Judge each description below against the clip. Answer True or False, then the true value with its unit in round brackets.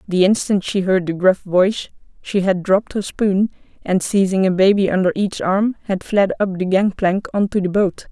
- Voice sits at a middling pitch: False (195 Hz)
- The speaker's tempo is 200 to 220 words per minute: True (205 wpm)